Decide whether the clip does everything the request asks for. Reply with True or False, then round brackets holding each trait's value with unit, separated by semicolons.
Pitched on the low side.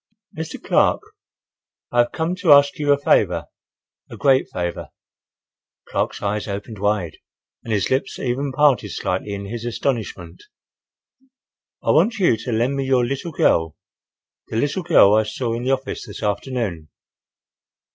True (120 Hz)